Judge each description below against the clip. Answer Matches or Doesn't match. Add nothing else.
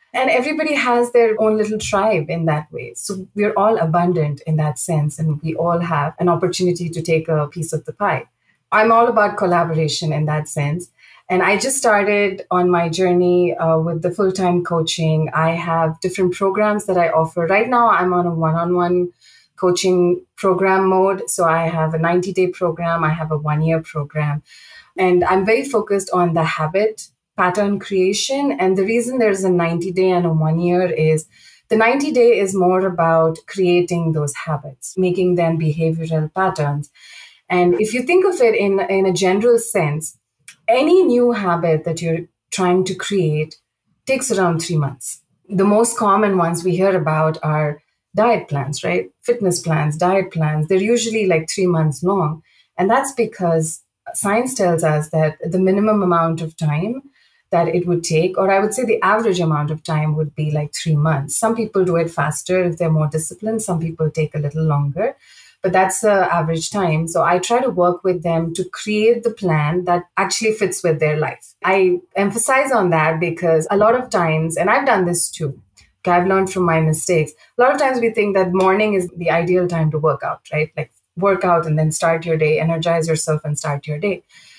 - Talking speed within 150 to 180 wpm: Doesn't match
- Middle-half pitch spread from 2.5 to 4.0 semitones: Matches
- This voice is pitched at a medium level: Matches